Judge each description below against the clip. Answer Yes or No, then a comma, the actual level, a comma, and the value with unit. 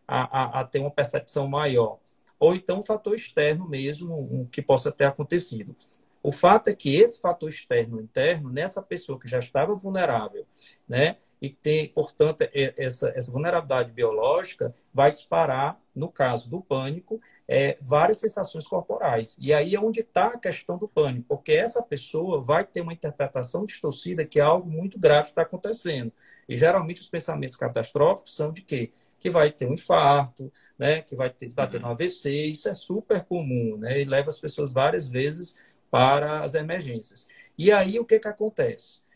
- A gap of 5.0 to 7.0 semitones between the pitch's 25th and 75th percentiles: Yes, average, 5.3 semitones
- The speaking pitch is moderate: Yes, medium, 150 Hz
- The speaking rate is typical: Yes, average, 175 wpm